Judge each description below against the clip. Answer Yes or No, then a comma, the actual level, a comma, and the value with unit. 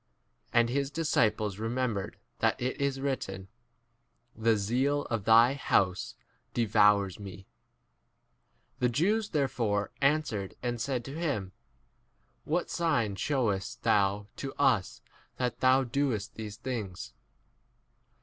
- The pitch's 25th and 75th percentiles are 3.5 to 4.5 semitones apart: No, average, 4.9 semitones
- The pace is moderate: No, slow, 120 wpm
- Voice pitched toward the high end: No, low, 120 Hz